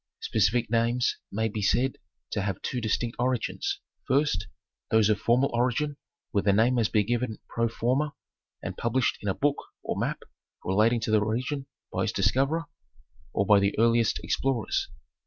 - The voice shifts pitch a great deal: No, average, 3.1 semitones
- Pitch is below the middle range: Yes, low, 115 Hz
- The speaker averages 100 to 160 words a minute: No, average, 170 wpm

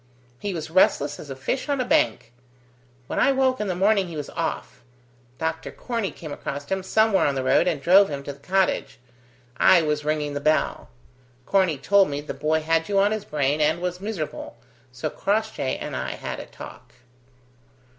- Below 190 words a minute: No, average, 195 wpm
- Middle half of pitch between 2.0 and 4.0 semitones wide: No, average, 5.0 semitones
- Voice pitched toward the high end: No, medium, 165 Hz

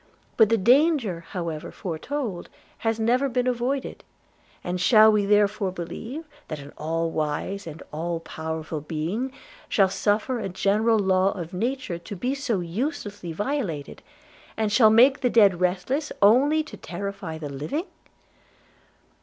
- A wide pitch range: Yes, wide, 6.1 semitones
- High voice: Yes, high, 200 Hz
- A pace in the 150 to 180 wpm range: No, average, 140 wpm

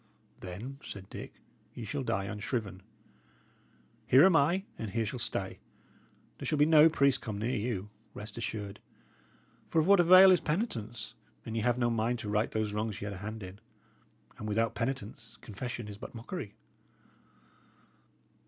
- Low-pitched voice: Yes, low, 115 Hz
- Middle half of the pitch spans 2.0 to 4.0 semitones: No, average, 4.6 semitones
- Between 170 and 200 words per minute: No, average, 160 wpm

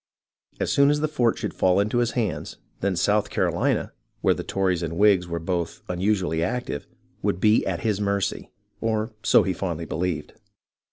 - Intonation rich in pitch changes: No, average, 3.7 semitones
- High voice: No, very low, 95 Hz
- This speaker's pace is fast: No, average, 175 wpm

